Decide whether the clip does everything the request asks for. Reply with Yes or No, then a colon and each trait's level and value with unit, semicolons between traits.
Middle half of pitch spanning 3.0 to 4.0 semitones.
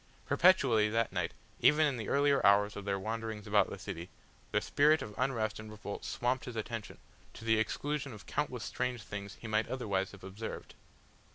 Yes: average, 3.7 semitones